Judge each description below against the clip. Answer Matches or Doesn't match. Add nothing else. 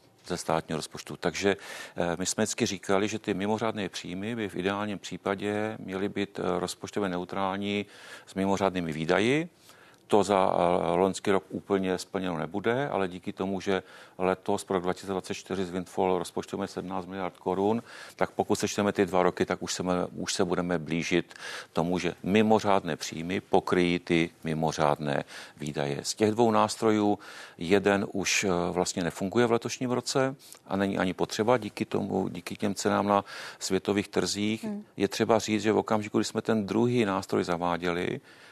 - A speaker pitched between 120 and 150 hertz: Doesn't match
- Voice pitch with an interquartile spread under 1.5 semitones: Doesn't match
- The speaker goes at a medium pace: Matches